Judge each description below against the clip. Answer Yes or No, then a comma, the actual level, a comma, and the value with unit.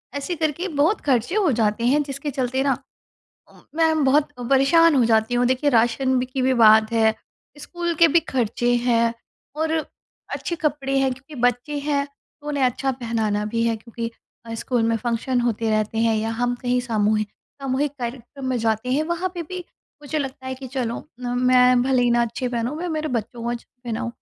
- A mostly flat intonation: No, average, 3.6 semitones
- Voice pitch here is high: Yes, very high, 250 Hz